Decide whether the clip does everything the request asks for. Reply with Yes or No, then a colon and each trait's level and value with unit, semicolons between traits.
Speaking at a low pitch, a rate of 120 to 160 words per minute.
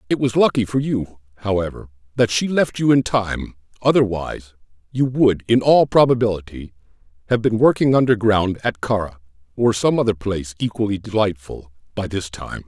Yes: low, 105 Hz; average, 155 wpm